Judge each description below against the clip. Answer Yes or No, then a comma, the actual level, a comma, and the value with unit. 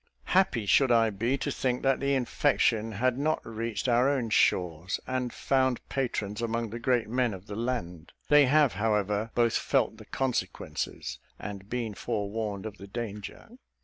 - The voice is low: Yes, low, 115 Hz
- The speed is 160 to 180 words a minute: Yes, average, 165 wpm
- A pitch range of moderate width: Yes, average, 3.5 semitones